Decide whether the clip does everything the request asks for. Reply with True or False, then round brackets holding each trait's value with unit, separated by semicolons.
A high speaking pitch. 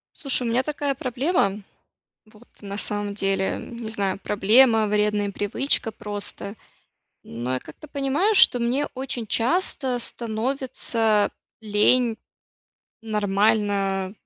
True (220 Hz)